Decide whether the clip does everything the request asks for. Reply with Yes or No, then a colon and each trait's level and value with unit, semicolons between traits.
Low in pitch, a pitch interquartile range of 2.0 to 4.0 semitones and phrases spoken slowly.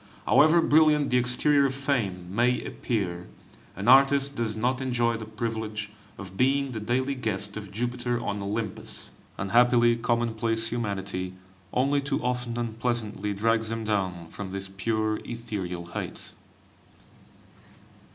Yes: low, 115 Hz; average, 3.3 semitones; slow, 130 wpm